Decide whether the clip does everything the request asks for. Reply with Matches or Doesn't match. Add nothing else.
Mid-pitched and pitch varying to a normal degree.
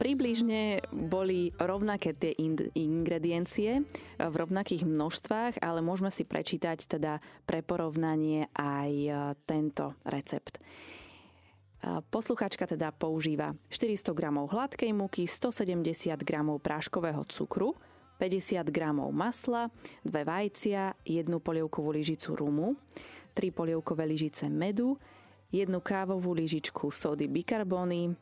Matches